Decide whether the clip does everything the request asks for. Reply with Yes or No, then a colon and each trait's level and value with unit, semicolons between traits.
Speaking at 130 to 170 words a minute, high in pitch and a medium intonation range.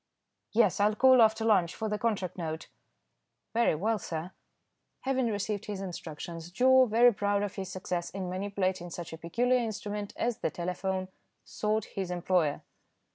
Yes: average, 155 wpm; high, 200 Hz; average, 3.7 semitones